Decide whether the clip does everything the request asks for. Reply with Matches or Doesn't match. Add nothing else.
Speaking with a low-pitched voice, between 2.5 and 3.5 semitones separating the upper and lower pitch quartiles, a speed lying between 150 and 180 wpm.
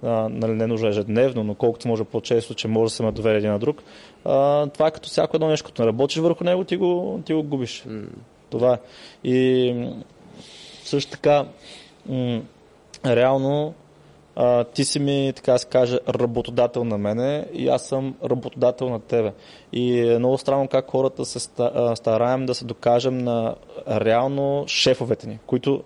Matches